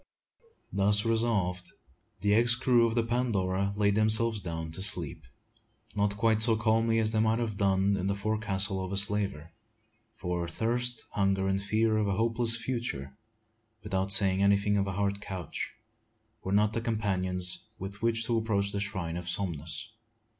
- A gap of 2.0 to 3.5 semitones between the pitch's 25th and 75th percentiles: Yes, average, 2.8 semitones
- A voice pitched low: Yes, low, 100 Hz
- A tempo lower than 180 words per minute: Yes, average, 165 wpm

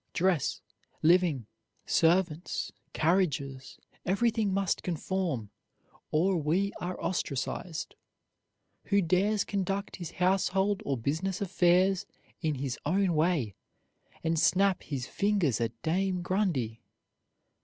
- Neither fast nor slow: No, slow, 100 wpm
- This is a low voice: No, medium, 180 Hz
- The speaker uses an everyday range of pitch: Yes, average, 4.1 semitones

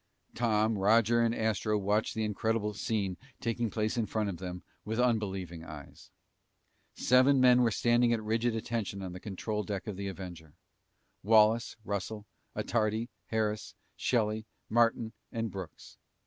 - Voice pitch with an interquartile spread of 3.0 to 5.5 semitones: No, narrow, 2.5 semitones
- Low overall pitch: Yes, low, 110 Hz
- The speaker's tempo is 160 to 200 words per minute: No, average, 145 wpm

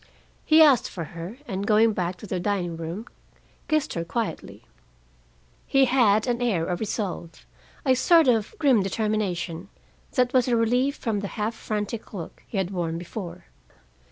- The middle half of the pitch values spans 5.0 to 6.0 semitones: Yes, average, 5.3 semitones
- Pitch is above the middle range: Yes, high, 210 Hz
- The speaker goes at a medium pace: Yes, average, 160 wpm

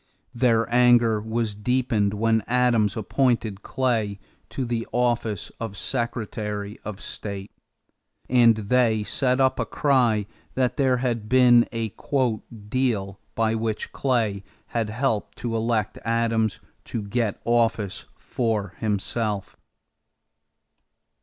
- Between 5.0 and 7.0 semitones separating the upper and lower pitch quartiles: No, narrow, 2.6 semitones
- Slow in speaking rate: Yes, slow, 115 wpm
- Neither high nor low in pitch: No, low, 115 Hz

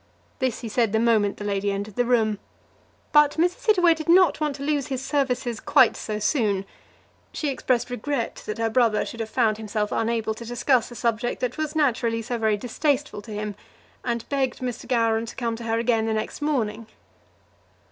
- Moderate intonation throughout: Yes, average, 3.5 semitones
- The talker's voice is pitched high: Yes, high, 235 Hz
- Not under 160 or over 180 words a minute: No, average, 195 wpm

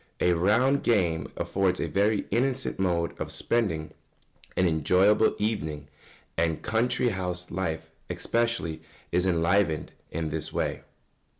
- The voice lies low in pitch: Yes, very low, 95 Hz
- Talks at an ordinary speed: No, slow, 130 wpm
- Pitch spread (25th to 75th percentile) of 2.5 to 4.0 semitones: No, average, 4.9 semitones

